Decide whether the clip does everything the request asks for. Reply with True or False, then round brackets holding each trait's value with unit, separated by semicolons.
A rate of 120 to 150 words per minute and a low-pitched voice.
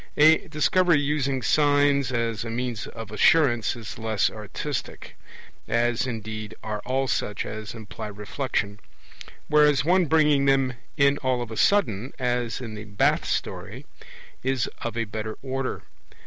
True (145 wpm; 125 Hz)